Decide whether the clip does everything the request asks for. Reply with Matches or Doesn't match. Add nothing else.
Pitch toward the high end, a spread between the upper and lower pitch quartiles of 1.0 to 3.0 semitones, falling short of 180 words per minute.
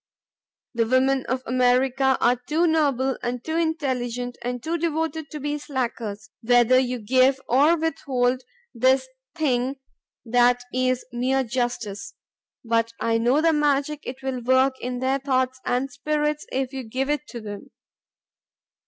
Matches